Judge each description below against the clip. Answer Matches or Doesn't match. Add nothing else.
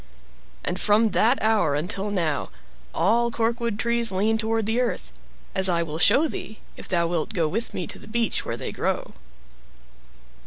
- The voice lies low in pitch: Doesn't match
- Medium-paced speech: Matches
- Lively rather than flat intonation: Doesn't match